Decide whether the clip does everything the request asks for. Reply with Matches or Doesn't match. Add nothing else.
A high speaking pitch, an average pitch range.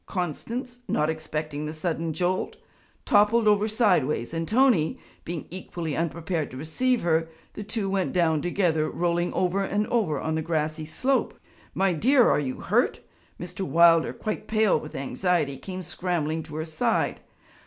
Doesn't match